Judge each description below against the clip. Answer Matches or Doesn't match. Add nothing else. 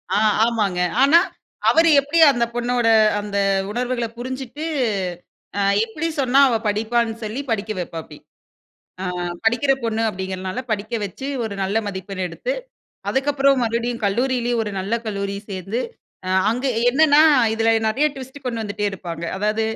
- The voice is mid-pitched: Doesn't match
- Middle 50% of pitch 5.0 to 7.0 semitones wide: Doesn't match